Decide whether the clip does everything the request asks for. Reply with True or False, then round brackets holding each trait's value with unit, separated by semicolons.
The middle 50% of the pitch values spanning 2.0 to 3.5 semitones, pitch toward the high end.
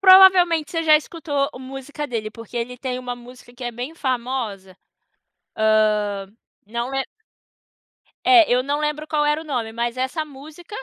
False (4.3 semitones; 260 Hz)